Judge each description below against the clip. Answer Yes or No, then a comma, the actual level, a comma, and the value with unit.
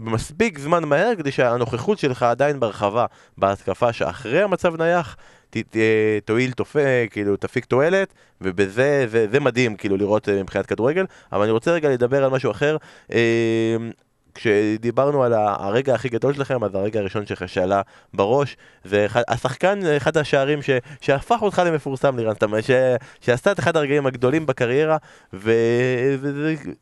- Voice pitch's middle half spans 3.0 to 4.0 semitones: No, average, 4.9 semitones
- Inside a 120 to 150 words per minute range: Yes, average, 145 wpm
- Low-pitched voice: Yes, low, 125 Hz